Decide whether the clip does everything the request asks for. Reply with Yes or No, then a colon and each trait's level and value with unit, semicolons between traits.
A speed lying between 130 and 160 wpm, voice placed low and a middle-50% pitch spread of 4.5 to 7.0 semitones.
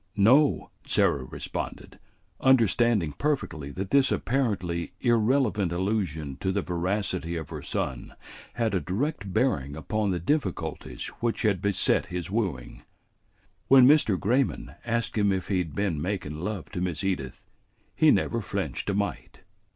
Yes: average, 145 wpm; very low, 95 Hz; average, 5.1 semitones